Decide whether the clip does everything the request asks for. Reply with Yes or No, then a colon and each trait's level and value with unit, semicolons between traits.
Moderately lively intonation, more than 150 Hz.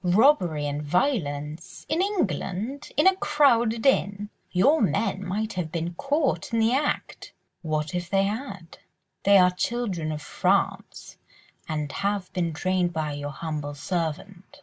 No: wide, 6.3 semitones; medium, 185 Hz